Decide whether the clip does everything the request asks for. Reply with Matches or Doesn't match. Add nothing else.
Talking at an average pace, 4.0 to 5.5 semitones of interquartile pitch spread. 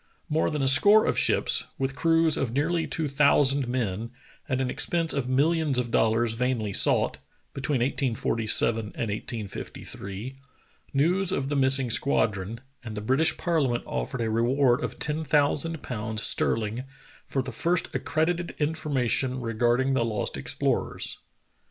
Matches